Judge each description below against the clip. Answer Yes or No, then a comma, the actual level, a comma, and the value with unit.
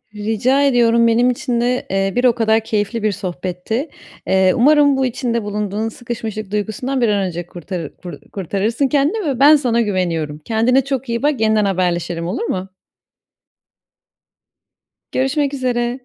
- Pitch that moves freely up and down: No, average, 4.6 semitones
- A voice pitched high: Yes, high, 225 Hz